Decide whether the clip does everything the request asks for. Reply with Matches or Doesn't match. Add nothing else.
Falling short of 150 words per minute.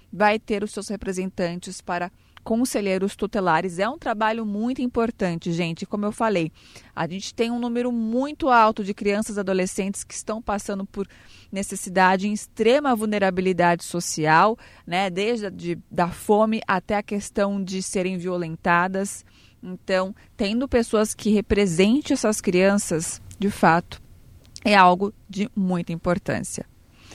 Matches